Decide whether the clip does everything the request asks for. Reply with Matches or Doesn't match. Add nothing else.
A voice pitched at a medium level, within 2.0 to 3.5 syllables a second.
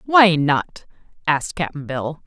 Matches